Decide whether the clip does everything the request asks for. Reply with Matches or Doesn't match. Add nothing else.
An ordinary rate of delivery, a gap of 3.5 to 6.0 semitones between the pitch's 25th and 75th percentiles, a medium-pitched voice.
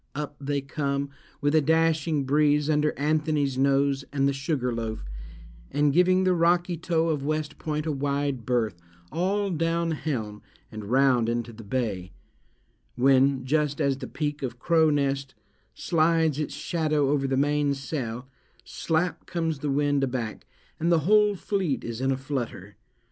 Doesn't match